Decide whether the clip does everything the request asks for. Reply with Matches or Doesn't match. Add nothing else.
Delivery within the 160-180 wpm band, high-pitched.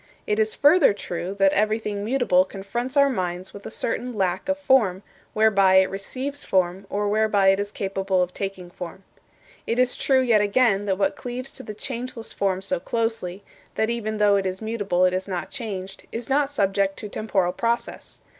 Doesn't match